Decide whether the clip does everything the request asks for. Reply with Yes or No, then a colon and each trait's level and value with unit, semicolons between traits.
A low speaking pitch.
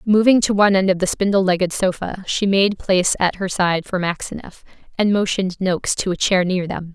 No: high, 190 Hz